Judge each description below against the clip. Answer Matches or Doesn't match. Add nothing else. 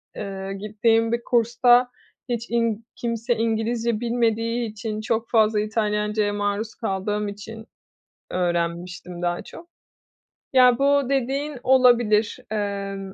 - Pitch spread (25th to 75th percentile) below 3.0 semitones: Matches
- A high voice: Matches